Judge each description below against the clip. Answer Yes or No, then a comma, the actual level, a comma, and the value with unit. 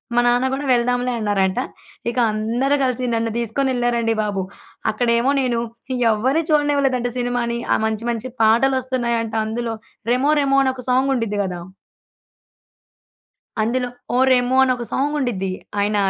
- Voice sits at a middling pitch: No, high, 245 Hz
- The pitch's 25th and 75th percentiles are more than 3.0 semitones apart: No, narrow, 2.4 semitones